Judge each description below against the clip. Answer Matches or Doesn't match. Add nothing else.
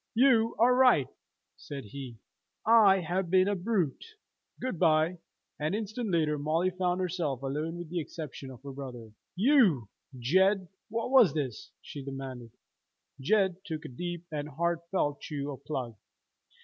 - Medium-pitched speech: Matches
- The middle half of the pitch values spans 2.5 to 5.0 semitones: Doesn't match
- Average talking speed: Matches